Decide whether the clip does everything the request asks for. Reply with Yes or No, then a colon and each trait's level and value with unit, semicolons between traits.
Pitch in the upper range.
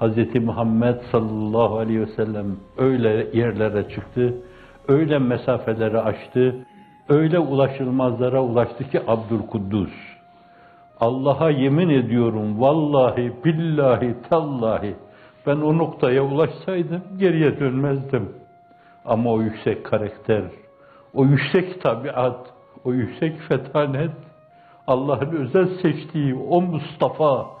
No: low, 130 Hz